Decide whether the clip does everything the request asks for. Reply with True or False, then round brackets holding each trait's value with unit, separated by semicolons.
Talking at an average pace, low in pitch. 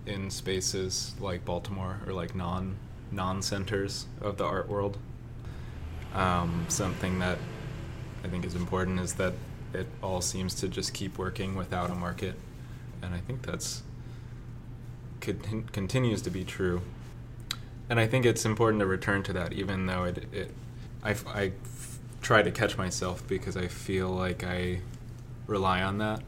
True (160 wpm; 100 Hz)